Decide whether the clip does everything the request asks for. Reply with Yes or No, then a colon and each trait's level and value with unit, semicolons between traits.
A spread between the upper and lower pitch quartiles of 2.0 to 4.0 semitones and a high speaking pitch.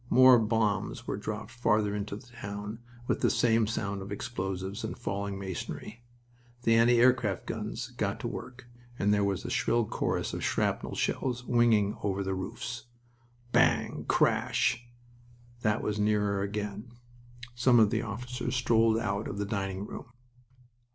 No: average, 2.8 semitones; low, 105 Hz